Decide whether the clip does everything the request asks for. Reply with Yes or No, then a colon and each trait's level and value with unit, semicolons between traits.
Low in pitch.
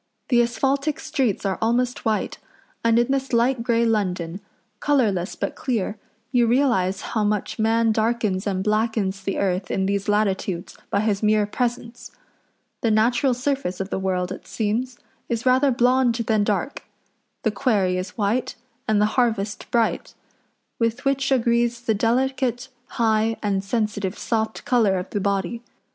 No: high, 225 Hz